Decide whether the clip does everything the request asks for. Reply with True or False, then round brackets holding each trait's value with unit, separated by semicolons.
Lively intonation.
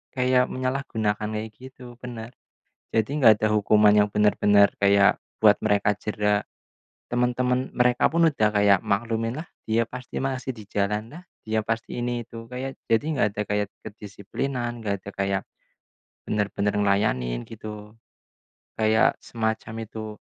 False (3.0 semitones)